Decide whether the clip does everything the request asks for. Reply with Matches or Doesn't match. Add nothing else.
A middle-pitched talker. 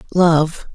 Matches